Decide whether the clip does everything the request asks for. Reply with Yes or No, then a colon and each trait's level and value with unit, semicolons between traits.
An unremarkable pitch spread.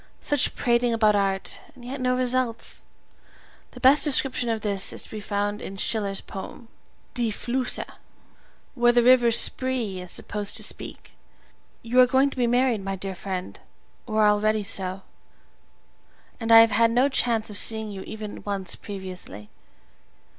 Yes: average, 3.4 semitones